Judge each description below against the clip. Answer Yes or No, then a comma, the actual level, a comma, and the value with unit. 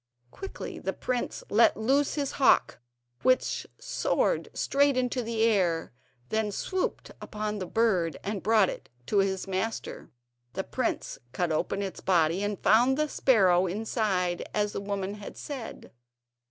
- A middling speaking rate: Yes, average, 150 wpm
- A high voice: Yes, high, 210 Hz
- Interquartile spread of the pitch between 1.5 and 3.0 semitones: No, average, 4.2 semitones